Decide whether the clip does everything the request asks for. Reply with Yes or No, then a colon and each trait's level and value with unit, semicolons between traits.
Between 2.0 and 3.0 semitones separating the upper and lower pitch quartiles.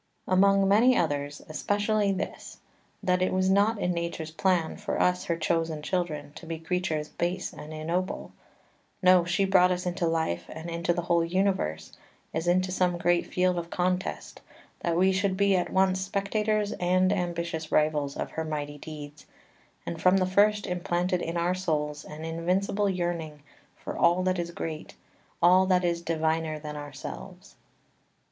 Yes: narrow, 2.6 semitones